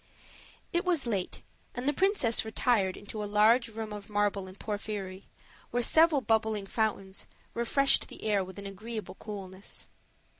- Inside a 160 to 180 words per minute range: No, average, 150 wpm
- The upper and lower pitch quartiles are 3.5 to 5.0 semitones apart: No, average, 3.0 semitones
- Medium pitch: No, high, 215 Hz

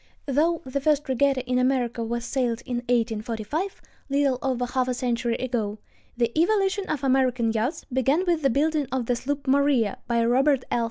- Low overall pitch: No, very high, 255 Hz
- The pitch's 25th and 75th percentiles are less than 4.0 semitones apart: Yes, average, 2.9 semitones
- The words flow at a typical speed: Yes, average, 175 wpm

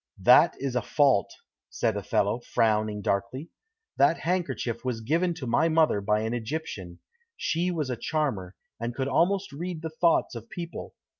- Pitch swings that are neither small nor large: No, wide, 6.8 semitones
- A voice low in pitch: Yes, low, 130 Hz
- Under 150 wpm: No, average, 160 wpm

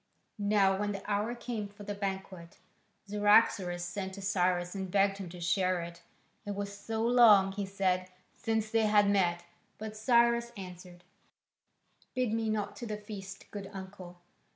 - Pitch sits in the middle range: No, high, 200 Hz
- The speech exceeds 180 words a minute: No, average, 160 wpm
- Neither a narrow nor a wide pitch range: No, narrow, 2.3 semitones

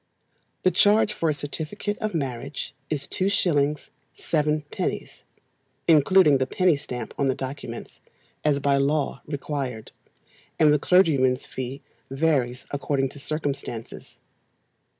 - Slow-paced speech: Yes, slow, 115 wpm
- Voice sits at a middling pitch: Yes, medium, 145 Hz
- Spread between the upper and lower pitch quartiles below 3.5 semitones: Yes, average, 2.9 semitones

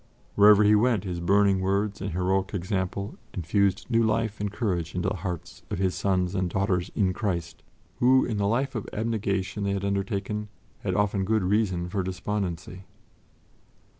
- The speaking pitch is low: Yes, low, 100 Hz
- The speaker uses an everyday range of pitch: No, narrow, 2.2 semitones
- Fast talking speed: No, average, 165 wpm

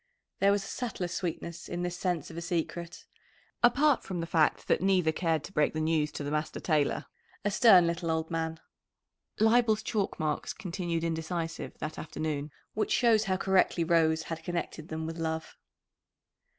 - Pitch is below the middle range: No, medium, 170 Hz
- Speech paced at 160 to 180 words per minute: Yes, average, 175 wpm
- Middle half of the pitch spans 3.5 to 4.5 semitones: No, average, 2.9 semitones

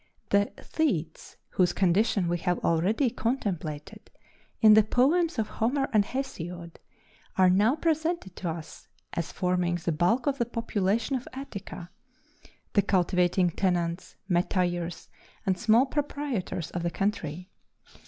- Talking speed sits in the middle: No, slow, 130 wpm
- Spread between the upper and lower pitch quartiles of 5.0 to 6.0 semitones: Yes, average, 5.3 semitones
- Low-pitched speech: No, high, 195 Hz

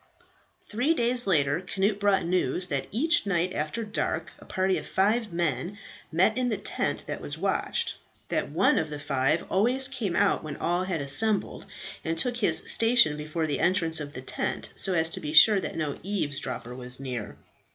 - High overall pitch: No, medium, 180 Hz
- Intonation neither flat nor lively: No, wide, 6.0 semitones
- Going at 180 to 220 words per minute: Yes, average, 185 wpm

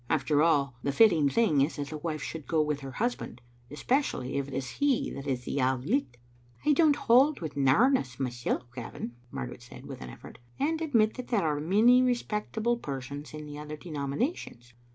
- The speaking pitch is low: No, medium, 150 Hz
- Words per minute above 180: Yes, average, 200 wpm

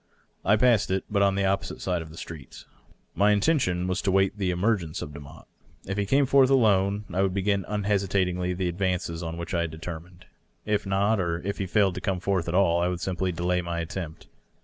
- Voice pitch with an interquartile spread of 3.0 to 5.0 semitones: No, narrow, 2.4 semitones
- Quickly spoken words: Yes, fast, 215 wpm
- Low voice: Yes, very low, 95 Hz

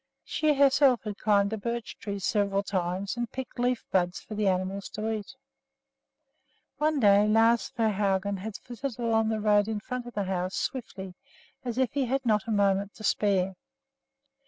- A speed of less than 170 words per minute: No, average, 175 wpm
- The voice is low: No, high, 215 Hz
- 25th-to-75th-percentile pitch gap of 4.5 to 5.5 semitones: No, average, 3.3 semitones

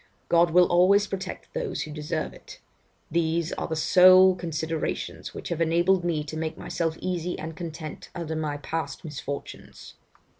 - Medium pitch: Yes, medium, 165 Hz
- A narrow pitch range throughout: Yes, narrow, 2.3 semitones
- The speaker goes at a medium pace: Yes, average, 155 wpm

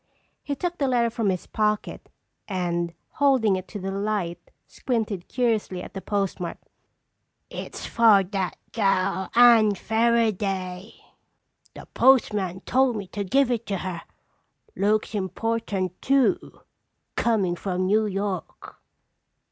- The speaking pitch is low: No, high, 205 Hz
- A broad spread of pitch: No, average, 3.7 semitones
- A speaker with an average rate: No, slow, 125 wpm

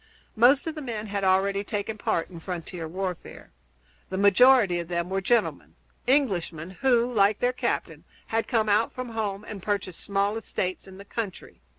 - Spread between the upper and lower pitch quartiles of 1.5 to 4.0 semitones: Yes, average, 3.5 semitones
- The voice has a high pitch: Yes, high, 200 Hz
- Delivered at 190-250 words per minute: No, average, 175 wpm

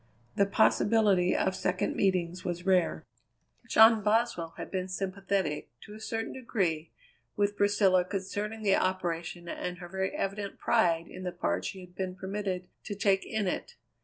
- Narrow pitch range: Yes, narrow, 2.3 semitones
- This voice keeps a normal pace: Yes, average, 160 wpm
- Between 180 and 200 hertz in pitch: Yes, high, 190 Hz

